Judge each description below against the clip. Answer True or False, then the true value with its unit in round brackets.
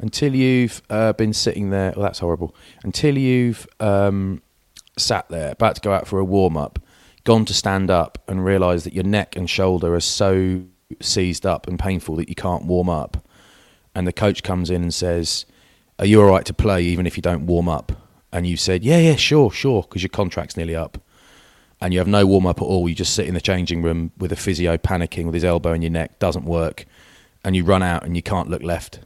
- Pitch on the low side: True (90 Hz)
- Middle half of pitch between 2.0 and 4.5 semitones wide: True (2.9 semitones)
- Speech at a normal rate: False (230 wpm)